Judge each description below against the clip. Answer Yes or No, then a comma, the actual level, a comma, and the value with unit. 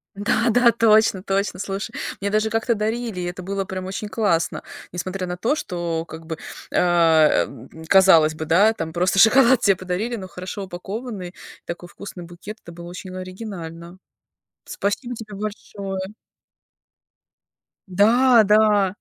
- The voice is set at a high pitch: Yes, high, 195 Hz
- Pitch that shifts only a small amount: No, average, 3.4 semitones